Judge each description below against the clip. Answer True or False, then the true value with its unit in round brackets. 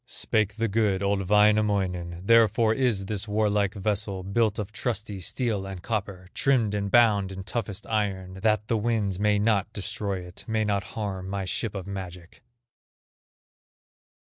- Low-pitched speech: True (105 Hz)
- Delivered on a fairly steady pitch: True (2.1 semitones)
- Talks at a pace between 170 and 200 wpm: False (150 wpm)